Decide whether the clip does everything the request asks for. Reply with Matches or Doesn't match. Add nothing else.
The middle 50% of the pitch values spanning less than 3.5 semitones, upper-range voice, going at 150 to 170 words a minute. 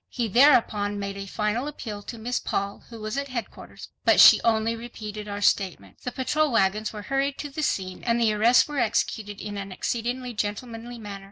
Doesn't match